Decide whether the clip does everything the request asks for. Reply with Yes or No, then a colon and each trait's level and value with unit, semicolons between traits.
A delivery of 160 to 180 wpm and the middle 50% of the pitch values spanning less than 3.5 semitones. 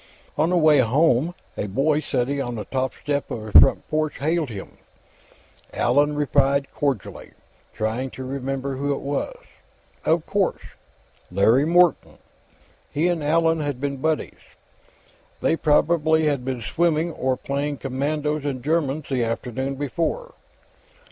No: average, 140 wpm; average, 3.1 semitones